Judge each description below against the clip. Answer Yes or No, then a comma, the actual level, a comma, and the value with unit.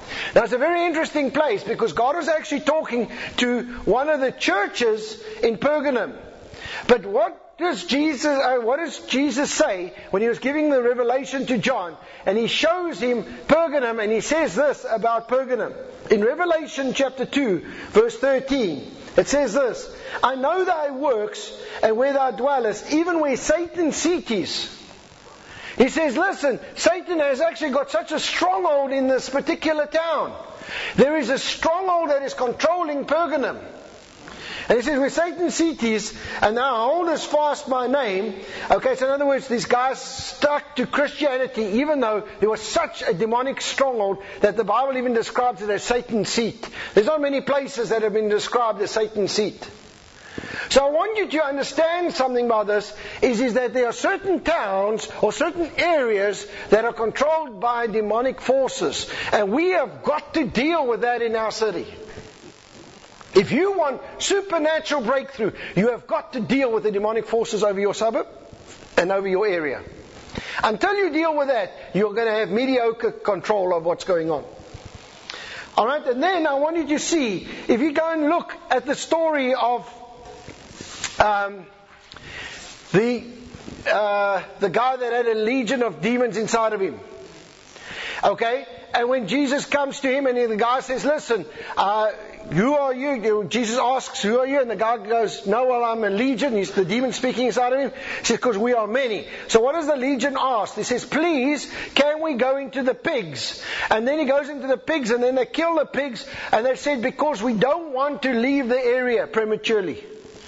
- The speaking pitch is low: No, very high, 260 Hz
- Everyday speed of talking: Yes, average, 180 wpm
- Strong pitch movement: No, average, 4.9 semitones